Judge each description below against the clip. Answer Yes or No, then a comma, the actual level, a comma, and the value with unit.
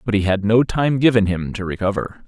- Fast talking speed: Yes, fast, 240 wpm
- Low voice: Yes, low, 105 Hz